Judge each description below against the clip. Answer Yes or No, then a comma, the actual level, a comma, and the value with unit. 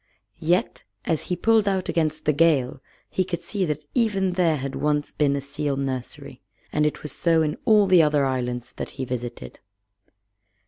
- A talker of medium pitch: Yes, medium, 150 Hz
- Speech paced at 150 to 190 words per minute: Yes, average, 180 wpm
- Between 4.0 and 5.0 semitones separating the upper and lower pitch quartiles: Yes, average, 4.5 semitones